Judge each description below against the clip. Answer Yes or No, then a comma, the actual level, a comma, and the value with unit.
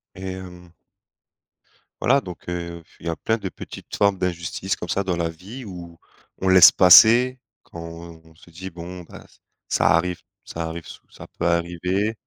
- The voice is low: Yes, very low, 90 Hz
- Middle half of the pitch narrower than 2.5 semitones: Yes, narrow, 2.1 semitones